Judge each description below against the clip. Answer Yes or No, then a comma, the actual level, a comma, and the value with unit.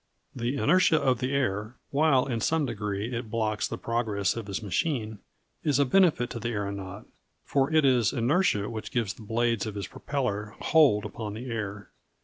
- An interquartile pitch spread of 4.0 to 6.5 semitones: Yes, average, 4.4 semitones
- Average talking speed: Yes, average, 180 wpm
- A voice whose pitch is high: No, low, 115 Hz